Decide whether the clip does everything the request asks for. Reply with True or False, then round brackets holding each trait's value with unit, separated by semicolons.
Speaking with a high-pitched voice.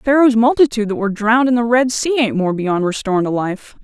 True (230 Hz)